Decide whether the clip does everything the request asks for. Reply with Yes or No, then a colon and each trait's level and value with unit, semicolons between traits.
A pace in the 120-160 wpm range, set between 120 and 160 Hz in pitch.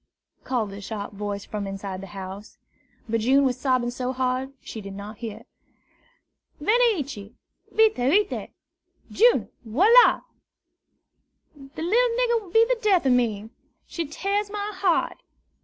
No: average, 140 wpm; very high, 260 Hz